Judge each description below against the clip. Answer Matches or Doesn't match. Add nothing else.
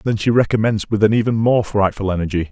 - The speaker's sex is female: Doesn't match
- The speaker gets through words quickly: Matches